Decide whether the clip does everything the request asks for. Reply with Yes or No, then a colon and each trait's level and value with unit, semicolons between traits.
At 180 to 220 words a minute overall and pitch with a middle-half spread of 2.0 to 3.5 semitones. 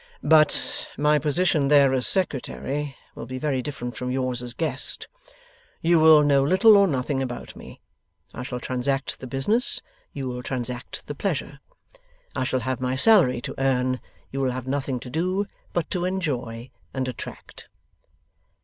No: average, 160 wpm; average, 3.2 semitones